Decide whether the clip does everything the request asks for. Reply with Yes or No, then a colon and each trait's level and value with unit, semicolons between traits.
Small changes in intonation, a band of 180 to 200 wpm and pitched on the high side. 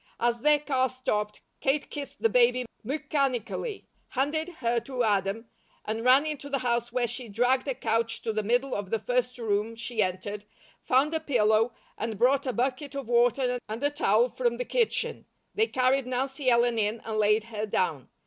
No: average, 3.2 semitones; average, 185 wpm; high, 245 Hz